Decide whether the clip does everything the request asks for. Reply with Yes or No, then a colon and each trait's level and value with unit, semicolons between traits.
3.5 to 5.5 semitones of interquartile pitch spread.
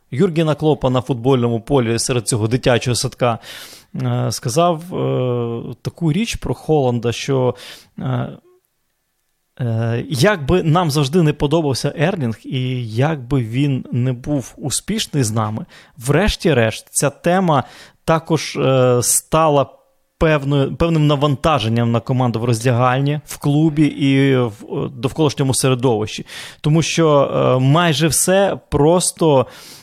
Yes: average, 3.9 semitones